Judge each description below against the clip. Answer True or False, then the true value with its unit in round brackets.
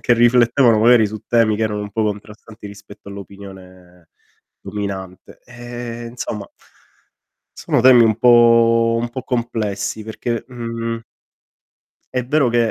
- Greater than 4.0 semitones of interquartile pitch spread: False (2.6 semitones)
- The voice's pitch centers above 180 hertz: False (115 Hz)